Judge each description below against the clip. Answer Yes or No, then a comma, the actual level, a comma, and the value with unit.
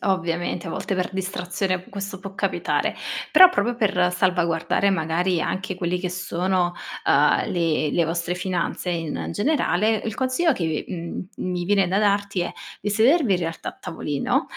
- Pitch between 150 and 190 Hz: Yes, medium, 185 Hz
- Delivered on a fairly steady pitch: Yes, narrow, 2.3 semitones